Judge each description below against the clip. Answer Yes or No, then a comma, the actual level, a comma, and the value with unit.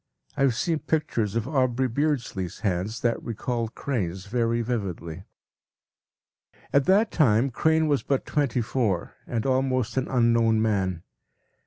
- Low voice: Yes, low, 120 Hz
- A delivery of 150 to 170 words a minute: No, slow, 135 wpm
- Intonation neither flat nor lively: Yes, average, 4.0 semitones